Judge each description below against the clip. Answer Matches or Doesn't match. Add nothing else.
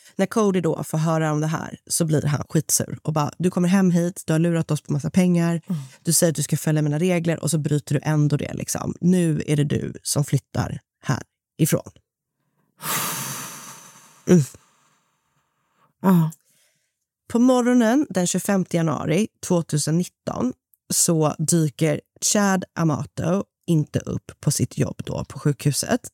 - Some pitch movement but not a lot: Matches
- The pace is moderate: Matches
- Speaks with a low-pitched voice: Doesn't match